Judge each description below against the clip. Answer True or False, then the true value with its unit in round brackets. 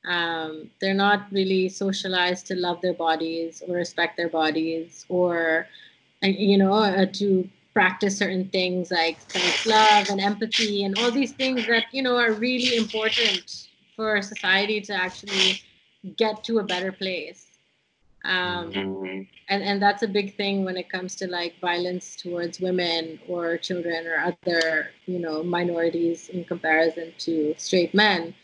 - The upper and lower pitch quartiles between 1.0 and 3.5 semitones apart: True (3.1 semitones)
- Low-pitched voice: False (185 Hz)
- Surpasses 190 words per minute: False (150 wpm)